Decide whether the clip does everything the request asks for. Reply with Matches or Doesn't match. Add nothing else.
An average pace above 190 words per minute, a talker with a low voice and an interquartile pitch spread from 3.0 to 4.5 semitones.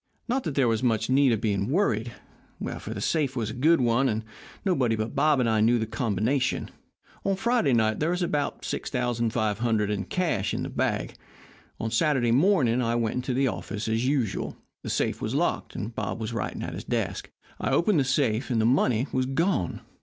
Matches